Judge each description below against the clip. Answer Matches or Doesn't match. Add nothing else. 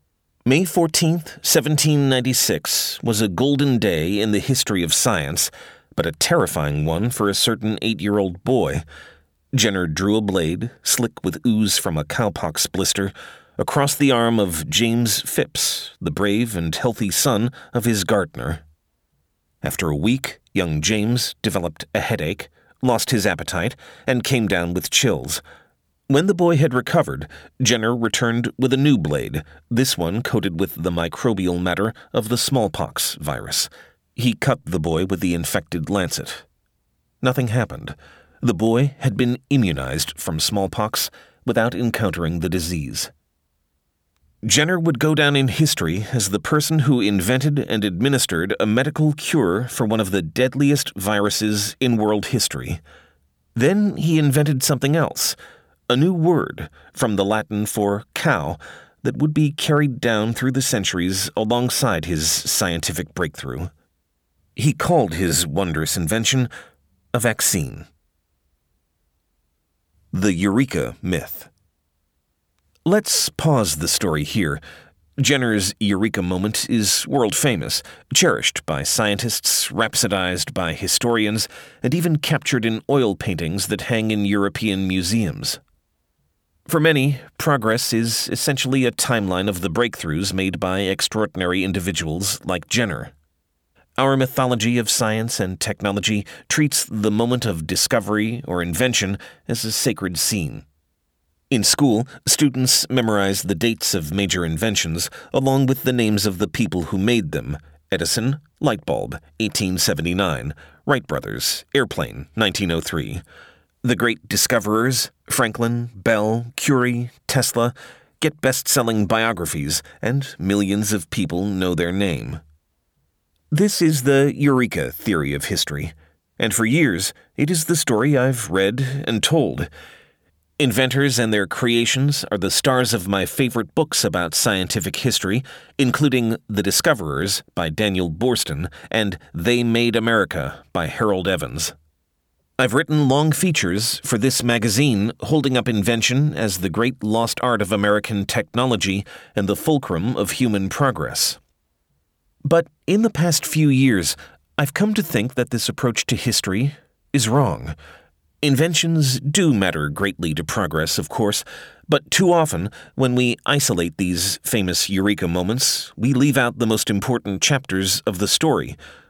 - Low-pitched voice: Matches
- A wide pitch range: Matches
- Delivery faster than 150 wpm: Doesn't match